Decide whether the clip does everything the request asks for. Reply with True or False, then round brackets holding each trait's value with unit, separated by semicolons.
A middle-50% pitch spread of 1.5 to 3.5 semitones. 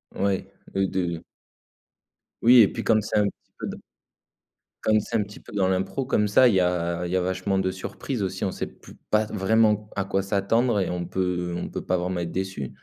True (2.4 semitones)